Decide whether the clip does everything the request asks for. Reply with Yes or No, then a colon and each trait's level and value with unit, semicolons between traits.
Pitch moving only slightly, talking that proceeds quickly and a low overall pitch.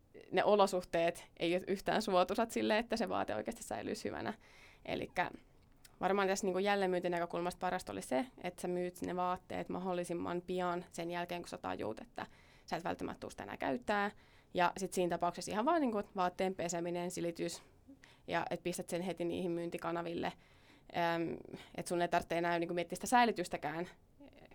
No: narrow, 1.6 semitones; fast, 170 wpm; medium, 180 Hz